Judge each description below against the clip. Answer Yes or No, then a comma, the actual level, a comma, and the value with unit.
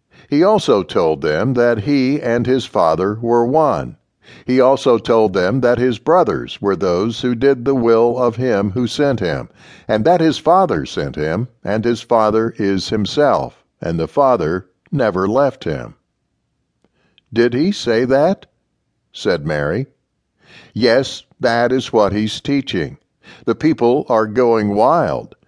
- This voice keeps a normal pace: Yes, average, 150 wpm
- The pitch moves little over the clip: No, average, 3.1 semitones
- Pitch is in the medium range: No, low, 120 Hz